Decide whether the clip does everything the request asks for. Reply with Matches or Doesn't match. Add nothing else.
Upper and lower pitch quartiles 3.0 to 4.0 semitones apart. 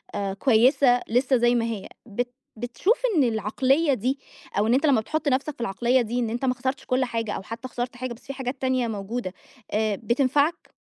Doesn't match